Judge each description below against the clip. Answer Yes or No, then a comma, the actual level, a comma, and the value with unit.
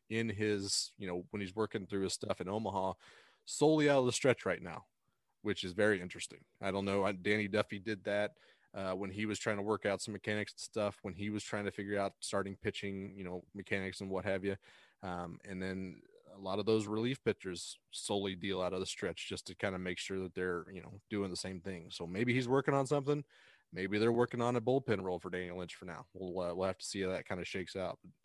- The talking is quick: Yes, fast, 245 wpm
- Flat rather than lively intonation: Yes, narrow, 2.3 semitones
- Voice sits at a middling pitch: No, low, 100 Hz